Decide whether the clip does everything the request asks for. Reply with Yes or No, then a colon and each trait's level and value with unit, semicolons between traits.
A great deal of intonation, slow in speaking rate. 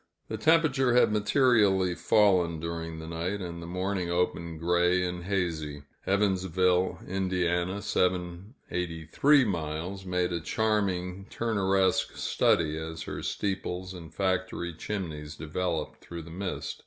No: narrow, 2.6 semitones; slow, 120 wpm